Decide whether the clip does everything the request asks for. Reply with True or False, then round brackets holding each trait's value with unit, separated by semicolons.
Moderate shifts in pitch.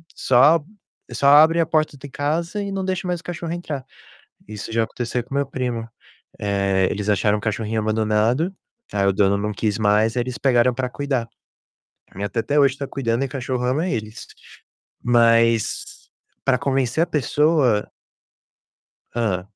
True (4.9 semitones)